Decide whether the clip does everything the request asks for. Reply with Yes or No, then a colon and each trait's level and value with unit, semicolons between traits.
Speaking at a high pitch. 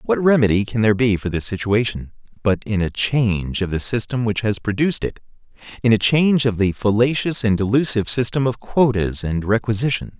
No: low, 110 Hz